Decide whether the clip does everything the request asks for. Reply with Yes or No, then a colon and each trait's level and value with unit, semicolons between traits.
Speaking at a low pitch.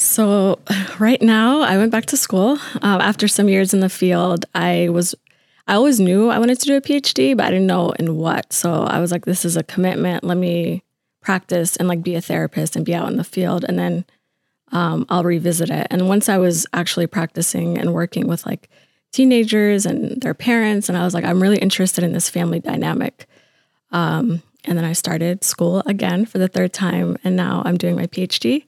No: medium, 180 Hz